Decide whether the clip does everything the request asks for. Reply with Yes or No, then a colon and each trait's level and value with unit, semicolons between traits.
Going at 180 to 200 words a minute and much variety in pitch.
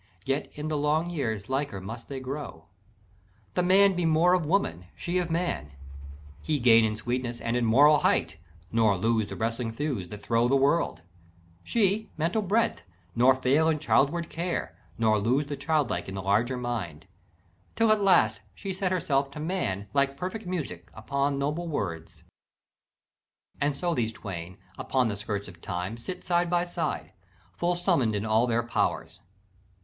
No: average, 170 wpm; wide, 7.2 semitones